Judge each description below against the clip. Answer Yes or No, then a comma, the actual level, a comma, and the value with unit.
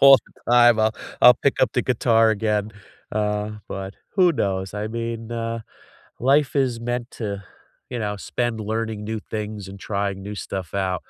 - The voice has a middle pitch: No, low, 110 Hz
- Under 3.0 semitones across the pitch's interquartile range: Yes, narrow, 2.5 semitones